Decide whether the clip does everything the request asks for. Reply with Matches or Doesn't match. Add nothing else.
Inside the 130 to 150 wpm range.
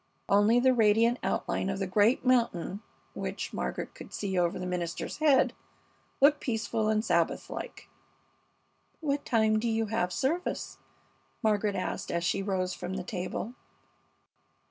Matches